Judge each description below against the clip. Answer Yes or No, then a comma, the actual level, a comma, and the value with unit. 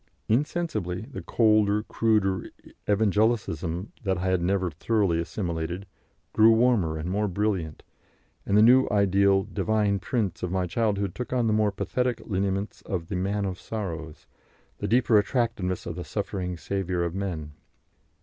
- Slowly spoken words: No, average, 145 wpm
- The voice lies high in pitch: No, low, 100 Hz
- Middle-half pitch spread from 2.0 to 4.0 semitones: Yes, average, 3.3 semitones